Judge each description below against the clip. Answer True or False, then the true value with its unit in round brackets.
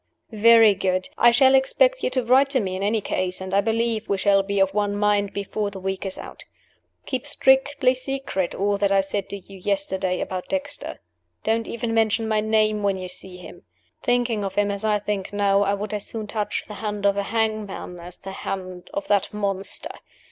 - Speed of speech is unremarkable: False (210 wpm)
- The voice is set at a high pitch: True (205 Hz)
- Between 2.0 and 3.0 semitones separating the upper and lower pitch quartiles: True (2.6 semitones)